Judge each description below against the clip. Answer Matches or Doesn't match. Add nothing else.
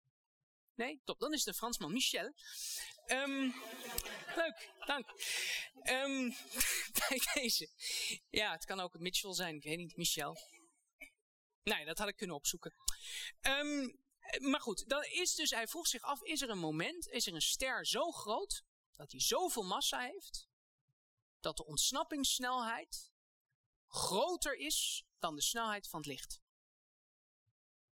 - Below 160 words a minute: Matches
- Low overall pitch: Doesn't match